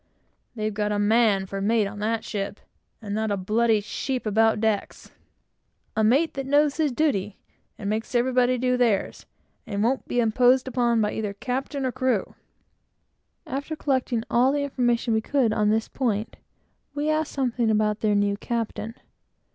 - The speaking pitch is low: No, high, 230 Hz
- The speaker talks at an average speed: Yes, average, 170 wpm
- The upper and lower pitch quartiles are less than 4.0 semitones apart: Yes, average, 3.4 semitones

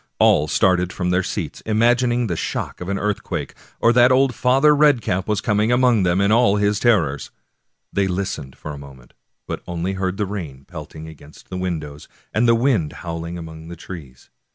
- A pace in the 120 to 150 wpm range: No, average, 195 wpm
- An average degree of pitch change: No, wide, 5.9 semitones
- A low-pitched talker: Yes, very low, 95 Hz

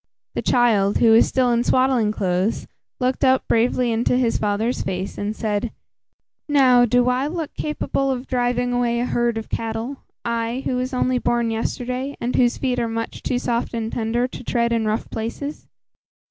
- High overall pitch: Yes, high, 240 Hz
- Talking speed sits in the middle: Yes, average, 180 wpm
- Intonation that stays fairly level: Yes, narrow, 2.0 semitones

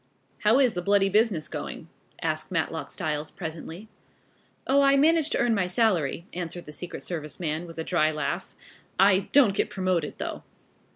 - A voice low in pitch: No, medium, 180 Hz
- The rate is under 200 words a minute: Yes, average, 170 wpm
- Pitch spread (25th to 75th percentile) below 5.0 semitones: No, average, 5.3 semitones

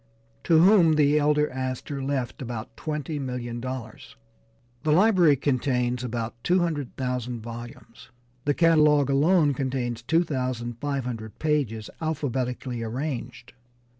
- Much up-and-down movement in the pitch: No, average, 3.7 semitones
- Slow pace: Yes, slow, 115 wpm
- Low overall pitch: Yes, low, 130 Hz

